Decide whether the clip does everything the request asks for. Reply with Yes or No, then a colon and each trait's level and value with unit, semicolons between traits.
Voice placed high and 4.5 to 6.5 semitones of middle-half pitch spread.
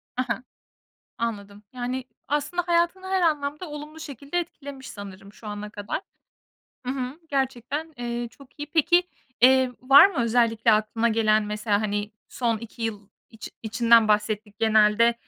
Yes: high, 235 Hz; average, 4.9 semitones